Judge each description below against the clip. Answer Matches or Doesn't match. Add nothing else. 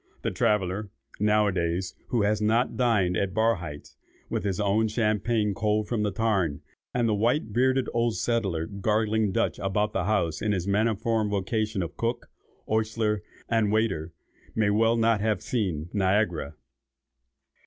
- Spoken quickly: Doesn't match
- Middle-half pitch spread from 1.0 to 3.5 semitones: Matches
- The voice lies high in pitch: Doesn't match